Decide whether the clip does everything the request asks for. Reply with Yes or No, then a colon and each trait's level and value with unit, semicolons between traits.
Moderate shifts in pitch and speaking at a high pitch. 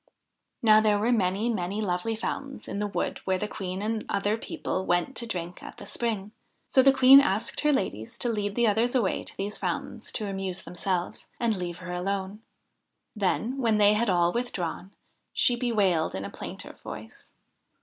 Yes: average, 3.8 semitones; high, 205 Hz